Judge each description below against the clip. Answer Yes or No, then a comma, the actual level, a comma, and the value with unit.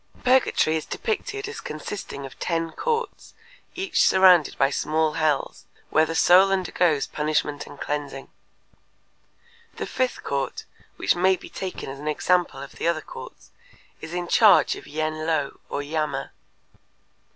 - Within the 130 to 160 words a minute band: Yes, average, 145 wpm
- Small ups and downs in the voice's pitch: No, average, 4.0 semitones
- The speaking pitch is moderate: Yes, medium, 160 Hz